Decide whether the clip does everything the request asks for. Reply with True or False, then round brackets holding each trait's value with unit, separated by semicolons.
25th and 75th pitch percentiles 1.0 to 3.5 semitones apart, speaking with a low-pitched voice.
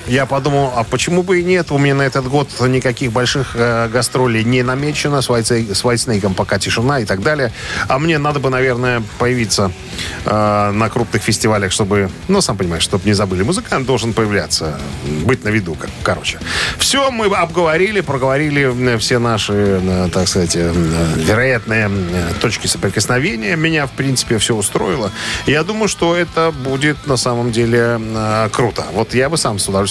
False (4.9 semitones; 120 Hz)